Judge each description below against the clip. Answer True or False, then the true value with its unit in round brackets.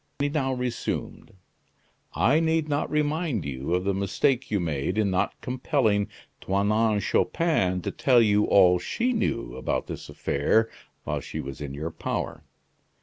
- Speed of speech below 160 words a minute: True (150 wpm)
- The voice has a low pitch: True (105 Hz)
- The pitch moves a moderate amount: False (7.6 semitones)